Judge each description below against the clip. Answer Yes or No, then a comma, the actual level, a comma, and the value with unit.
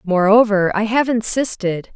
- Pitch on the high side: Yes, high, 210 Hz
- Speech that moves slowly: Yes, slow, 125 wpm